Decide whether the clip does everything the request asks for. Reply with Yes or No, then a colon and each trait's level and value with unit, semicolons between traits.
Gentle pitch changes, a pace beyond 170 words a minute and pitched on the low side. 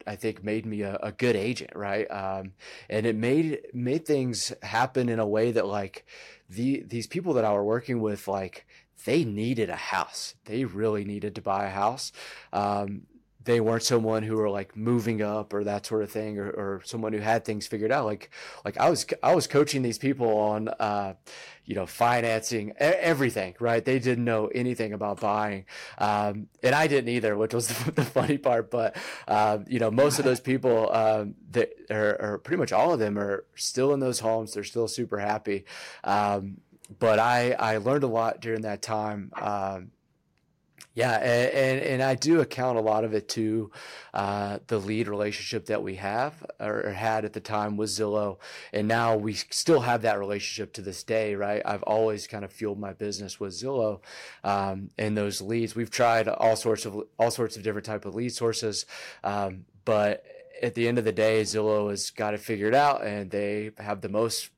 Yes: narrow, 2.3 semitones; average, 200 wpm; low, 110 Hz